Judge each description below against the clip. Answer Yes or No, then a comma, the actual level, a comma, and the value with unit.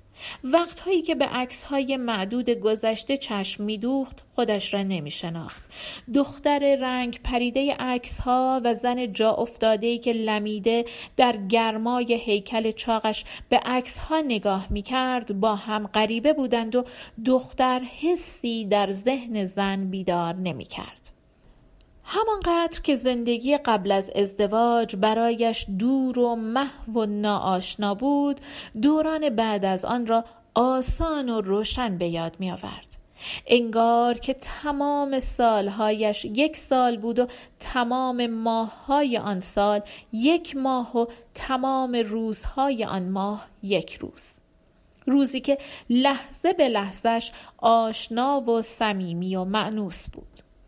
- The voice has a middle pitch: No, high, 235 Hz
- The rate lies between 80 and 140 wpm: Yes, average, 120 wpm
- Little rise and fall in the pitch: No, average, 3.6 semitones